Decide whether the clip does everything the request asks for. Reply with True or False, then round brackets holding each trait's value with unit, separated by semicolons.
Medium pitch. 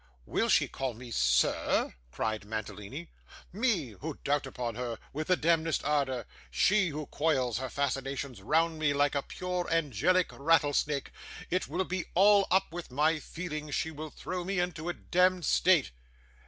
True (150 Hz)